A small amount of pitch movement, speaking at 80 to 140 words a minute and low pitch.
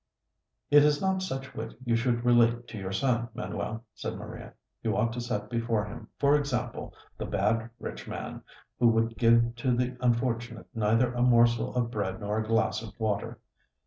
No: narrow, 1.7 semitones; average, 180 wpm; low, 115 Hz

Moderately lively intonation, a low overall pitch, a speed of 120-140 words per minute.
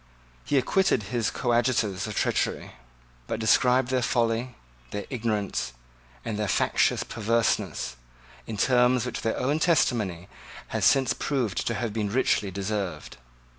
Yes: average, 3.4 semitones; low, 115 Hz; slow, 135 wpm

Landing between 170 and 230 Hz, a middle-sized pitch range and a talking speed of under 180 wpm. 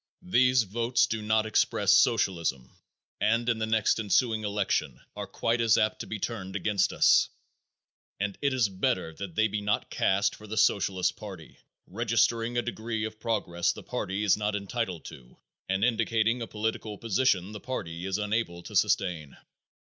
No: low, 110 Hz; average, 3.1 semitones; average, 170 wpm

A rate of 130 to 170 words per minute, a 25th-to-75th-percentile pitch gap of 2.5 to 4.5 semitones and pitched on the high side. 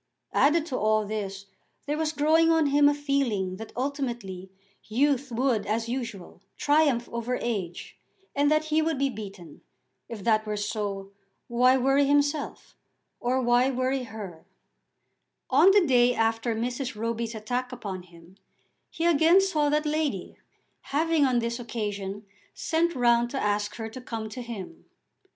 No: average, 150 wpm; average, 5.0 semitones; high, 245 Hz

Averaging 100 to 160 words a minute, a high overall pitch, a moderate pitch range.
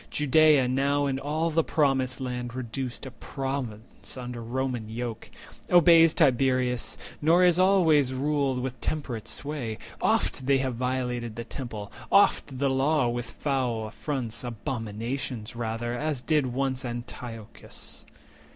No: slow, 135 wpm; low, 130 Hz; average, 3.2 semitones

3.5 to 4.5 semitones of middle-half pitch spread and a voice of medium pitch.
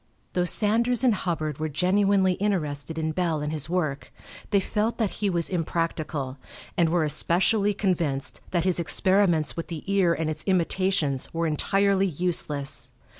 Yes: average, 4.0 semitones; medium, 175 Hz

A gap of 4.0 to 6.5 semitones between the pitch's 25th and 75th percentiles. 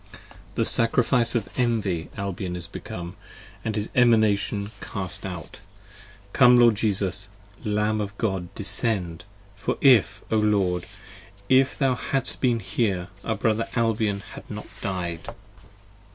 No: average, 3.3 semitones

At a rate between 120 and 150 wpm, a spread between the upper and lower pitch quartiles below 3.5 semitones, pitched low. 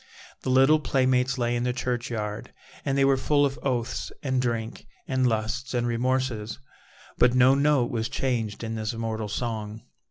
No: average, 165 wpm; narrow, 2.6 semitones; low, 125 Hz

